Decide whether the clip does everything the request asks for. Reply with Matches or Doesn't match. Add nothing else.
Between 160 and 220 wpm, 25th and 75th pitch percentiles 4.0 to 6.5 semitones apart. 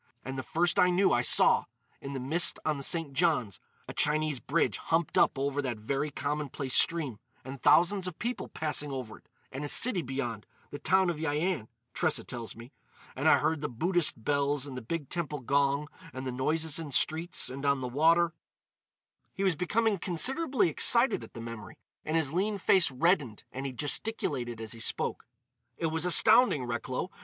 Matches